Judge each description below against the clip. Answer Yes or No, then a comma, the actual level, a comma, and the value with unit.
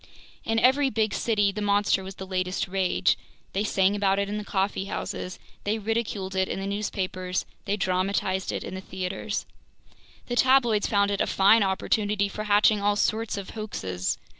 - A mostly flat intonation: Yes, narrow, 1.9 semitones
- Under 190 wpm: Yes, average, 180 wpm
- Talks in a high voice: Yes, high, 200 Hz